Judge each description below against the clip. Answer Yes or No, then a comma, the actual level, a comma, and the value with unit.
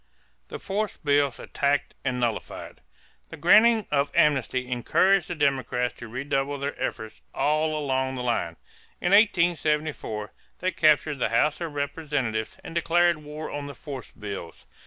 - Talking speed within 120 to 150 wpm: Yes, average, 145 wpm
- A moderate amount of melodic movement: Yes, average, 3.8 semitones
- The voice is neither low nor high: Yes, medium, 145 Hz